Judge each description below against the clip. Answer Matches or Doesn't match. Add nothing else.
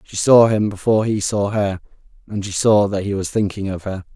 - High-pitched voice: Doesn't match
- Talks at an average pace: Doesn't match